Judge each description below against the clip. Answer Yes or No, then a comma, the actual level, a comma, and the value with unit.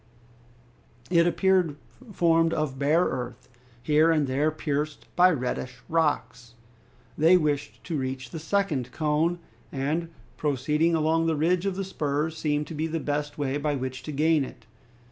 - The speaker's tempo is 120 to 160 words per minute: Yes, average, 155 wpm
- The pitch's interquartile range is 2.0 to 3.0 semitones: Yes, average, 2.7 semitones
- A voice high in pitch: No, medium, 150 Hz